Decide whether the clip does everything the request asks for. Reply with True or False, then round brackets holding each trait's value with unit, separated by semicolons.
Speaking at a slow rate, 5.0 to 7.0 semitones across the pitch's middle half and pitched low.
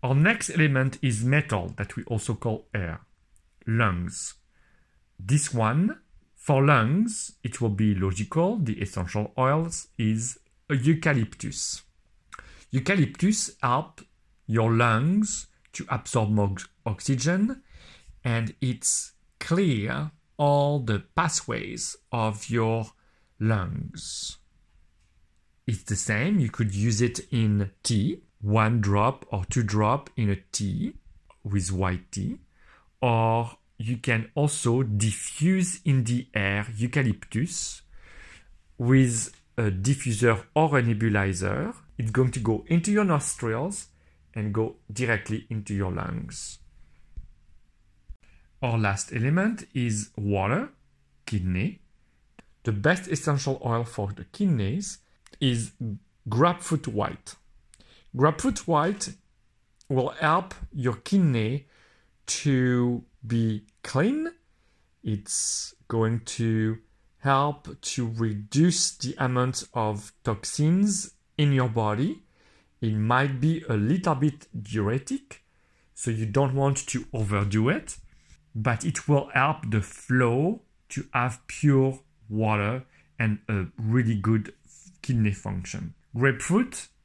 True (110 wpm; 5.3 semitones; 115 Hz)